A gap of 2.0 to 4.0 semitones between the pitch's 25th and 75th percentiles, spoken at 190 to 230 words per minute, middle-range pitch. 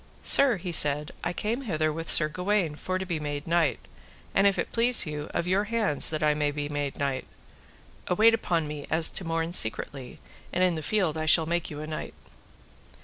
Yes: average, 3.7 semitones; fast, 205 wpm; medium, 165 Hz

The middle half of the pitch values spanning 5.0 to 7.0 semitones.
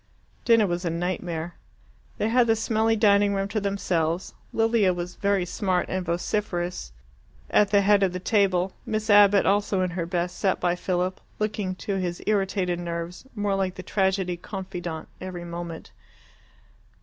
No: narrow, 2.6 semitones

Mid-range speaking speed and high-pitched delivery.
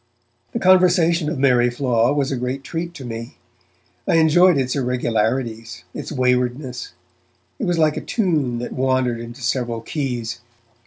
No: average, 150 wpm; low, 130 Hz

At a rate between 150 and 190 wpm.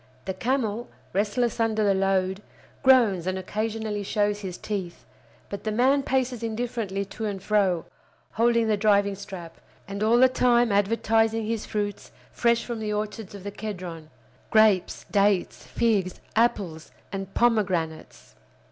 No: average, 140 wpm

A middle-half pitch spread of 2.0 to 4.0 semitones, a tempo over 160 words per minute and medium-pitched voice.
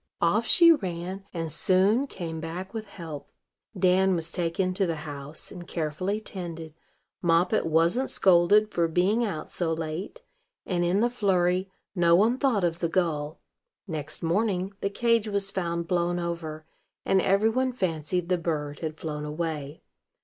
No: average, 3.3 semitones; average, 155 wpm; medium, 175 Hz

